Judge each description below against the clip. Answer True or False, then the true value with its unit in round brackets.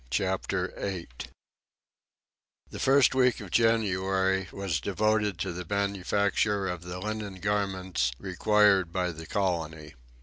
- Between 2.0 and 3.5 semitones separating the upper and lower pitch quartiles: True (2.5 semitones)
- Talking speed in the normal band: False (115 wpm)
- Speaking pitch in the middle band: False (95 Hz)